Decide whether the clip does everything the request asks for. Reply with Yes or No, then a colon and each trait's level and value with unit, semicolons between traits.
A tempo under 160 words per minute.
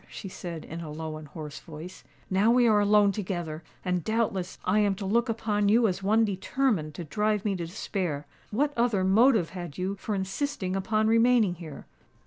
No: average, 185 wpm